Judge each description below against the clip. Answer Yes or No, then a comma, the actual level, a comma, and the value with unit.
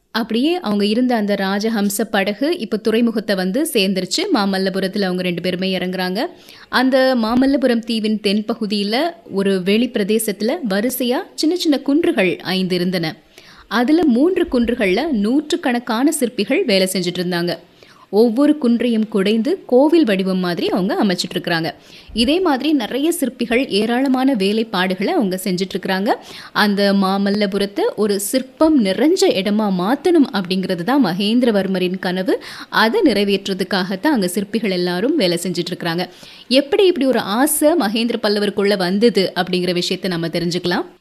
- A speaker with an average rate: Yes, average, 120 wpm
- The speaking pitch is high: Yes, high, 210 Hz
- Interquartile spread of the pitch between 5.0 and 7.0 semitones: Yes, wide, 5.4 semitones